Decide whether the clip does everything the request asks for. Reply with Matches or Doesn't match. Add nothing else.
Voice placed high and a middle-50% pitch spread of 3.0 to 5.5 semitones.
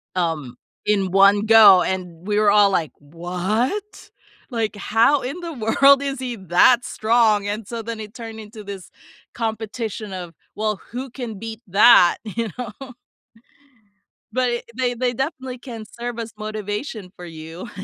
Matches